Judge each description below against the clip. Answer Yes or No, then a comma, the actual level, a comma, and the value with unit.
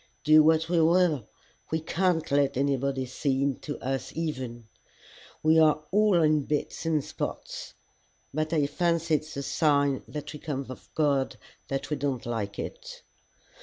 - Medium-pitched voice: Yes, medium, 150 Hz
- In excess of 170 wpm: No, average, 155 wpm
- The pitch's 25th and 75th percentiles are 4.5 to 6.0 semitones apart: No, average, 2.8 semitones